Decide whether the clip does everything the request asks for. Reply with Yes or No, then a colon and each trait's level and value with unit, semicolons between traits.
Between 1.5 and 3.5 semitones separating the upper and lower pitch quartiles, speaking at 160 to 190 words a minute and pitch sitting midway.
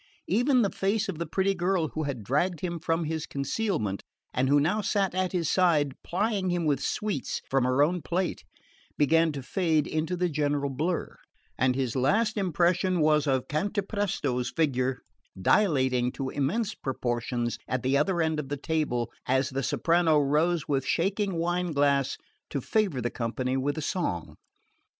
No: average, 5.2 semitones; average, 170 wpm; medium, 155 Hz